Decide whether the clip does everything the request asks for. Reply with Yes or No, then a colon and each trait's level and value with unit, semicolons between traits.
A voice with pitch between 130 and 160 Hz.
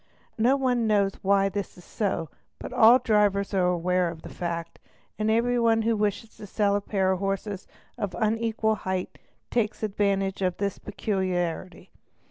No: high, 200 Hz